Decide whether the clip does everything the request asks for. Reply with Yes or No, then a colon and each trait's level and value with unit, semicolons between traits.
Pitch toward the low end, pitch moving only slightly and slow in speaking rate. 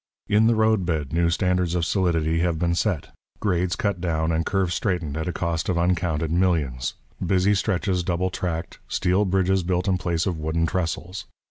No: very low, 90 Hz; narrow, 2.1 semitones; average, 185 wpm